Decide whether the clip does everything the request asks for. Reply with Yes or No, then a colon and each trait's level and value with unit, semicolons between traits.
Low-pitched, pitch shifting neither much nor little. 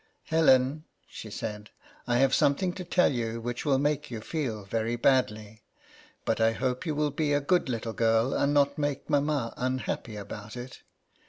Yes: low, 130 Hz; average, 4.3 semitones